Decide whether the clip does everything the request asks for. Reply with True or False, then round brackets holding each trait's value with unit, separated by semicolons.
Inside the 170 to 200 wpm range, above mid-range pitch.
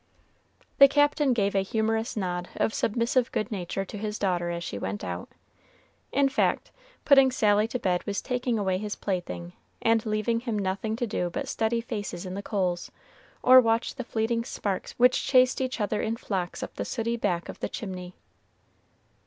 True (180 wpm; 215 Hz)